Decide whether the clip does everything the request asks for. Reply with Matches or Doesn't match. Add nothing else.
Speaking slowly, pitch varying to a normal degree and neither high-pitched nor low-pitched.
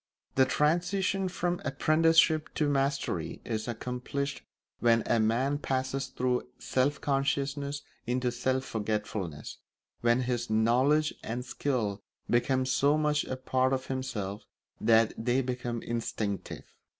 Doesn't match